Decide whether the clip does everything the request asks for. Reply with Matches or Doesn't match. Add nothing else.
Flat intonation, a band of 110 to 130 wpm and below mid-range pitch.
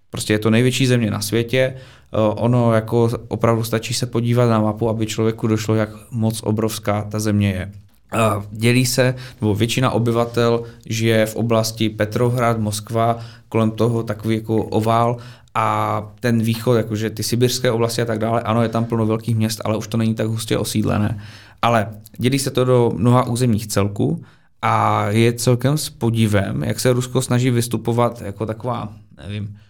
Doesn't match